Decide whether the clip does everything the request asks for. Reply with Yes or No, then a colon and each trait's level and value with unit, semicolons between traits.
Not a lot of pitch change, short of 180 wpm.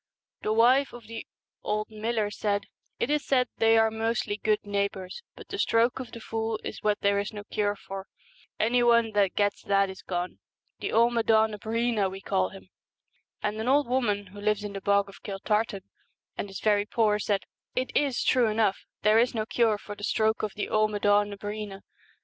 No: narrow, 2.0 semitones; average, 200 wpm